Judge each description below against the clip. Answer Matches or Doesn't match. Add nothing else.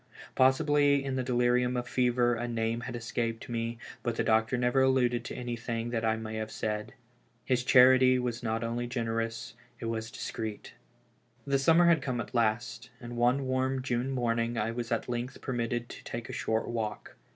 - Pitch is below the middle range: Matches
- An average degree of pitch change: Doesn't match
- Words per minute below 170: Doesn't match